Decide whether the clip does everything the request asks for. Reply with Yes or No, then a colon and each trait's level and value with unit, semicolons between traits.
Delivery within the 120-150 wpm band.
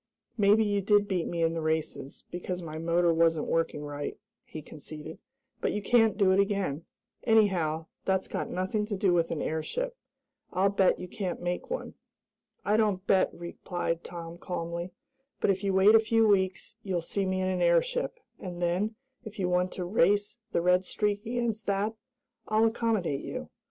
No: average, 180 wpm